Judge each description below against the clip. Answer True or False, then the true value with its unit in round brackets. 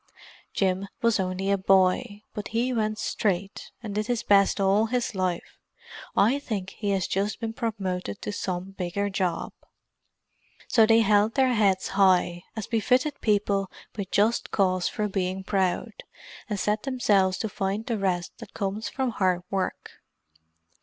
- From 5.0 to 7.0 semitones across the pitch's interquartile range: False (2.6 semitones)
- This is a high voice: True (200 Hz)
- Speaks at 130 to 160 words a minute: True (155 wpm)